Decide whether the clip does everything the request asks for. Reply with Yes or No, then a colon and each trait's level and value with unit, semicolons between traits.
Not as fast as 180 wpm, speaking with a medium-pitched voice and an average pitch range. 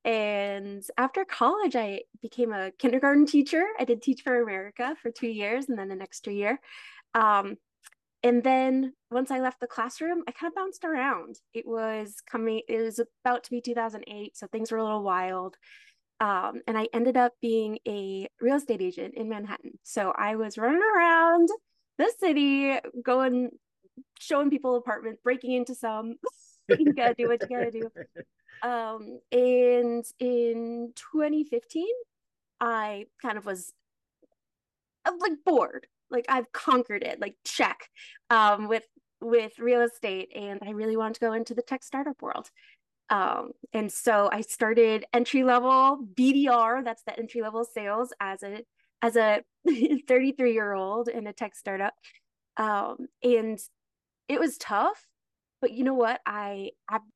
No: average, 160 wpm; high, 235 Hz; average, 3.2 semitones